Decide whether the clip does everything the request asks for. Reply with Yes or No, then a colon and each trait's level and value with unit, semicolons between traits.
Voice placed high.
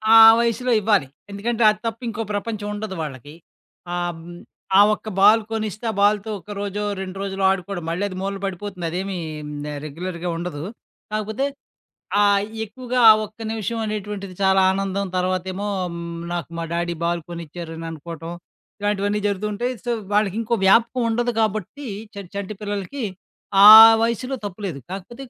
Yes: high, 200 Hz